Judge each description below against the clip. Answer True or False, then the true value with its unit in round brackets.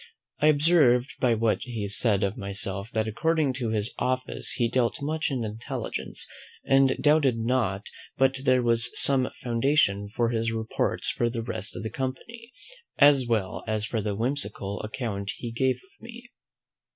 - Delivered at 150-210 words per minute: True (165 wpm)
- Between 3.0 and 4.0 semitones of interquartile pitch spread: True (3.7 semitones)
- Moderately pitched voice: False (120 Hz)